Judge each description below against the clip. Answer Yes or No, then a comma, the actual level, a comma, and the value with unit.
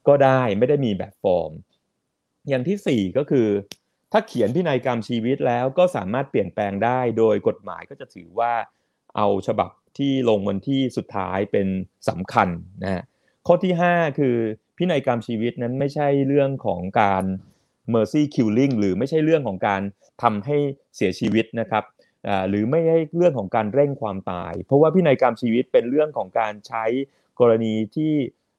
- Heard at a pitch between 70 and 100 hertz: No, low, 120 Hz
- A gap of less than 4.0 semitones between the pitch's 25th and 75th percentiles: No, wide, 5.4 semitones